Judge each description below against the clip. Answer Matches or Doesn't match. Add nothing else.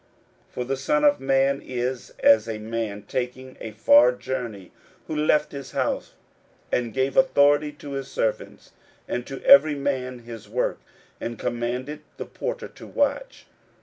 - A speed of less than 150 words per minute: Doesn't match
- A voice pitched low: Matches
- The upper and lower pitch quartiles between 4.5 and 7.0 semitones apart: Doesn't match